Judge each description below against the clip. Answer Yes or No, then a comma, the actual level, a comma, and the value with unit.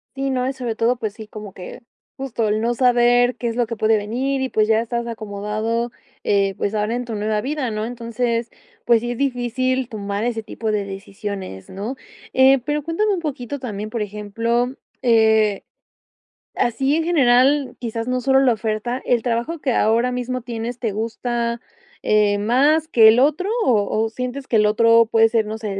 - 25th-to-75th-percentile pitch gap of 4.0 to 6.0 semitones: No, average, 2.7 semitones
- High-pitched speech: Yes, high, 235 Hz